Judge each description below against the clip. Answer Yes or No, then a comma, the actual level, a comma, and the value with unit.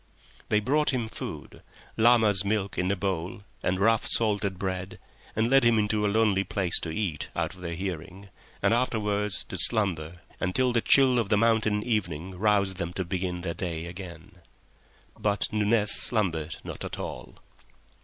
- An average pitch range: Yes, average, 3.3 semitones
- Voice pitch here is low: Yes, low, 100 Hz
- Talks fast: No, average, 165 wpm